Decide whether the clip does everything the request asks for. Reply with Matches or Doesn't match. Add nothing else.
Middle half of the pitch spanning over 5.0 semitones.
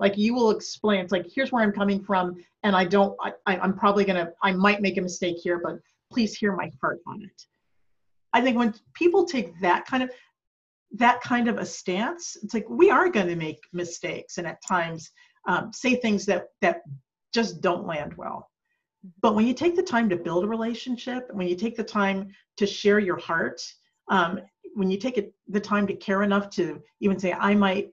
Doesn't match